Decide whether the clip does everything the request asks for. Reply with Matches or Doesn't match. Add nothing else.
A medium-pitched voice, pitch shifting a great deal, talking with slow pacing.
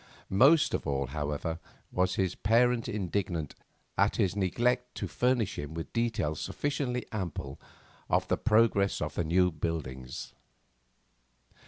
Doesn't match